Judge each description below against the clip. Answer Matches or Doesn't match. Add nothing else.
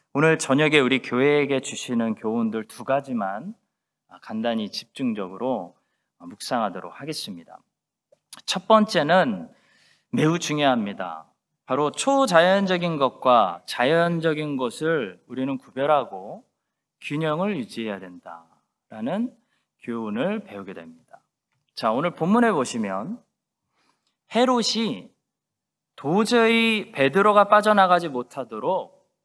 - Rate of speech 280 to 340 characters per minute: Doesn't match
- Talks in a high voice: Doesn't match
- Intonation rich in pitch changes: Matches